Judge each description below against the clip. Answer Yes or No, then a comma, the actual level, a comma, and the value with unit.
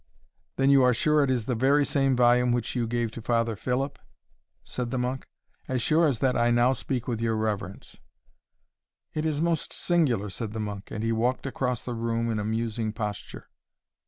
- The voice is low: Yes, low, 120 Hz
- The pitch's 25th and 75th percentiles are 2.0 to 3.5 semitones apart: Yes, average, 2.8 semitones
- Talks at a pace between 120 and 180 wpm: No, average, 195 wpm